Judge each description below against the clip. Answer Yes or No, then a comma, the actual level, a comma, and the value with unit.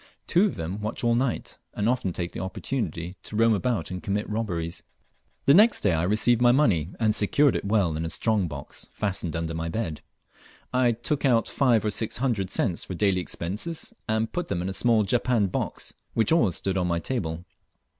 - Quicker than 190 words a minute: Yes, fast, 205 wpm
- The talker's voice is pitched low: Yes, low, 105 Hz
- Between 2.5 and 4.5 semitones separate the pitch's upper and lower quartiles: No, average, 5.2 semitones